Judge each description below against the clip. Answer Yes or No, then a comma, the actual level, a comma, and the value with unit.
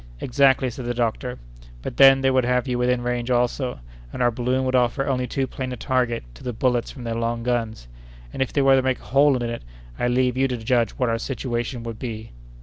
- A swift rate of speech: Yes, fast, 240 wpm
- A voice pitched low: Yes, low, 125 Hz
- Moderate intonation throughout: No, narrow, 1.7 semitones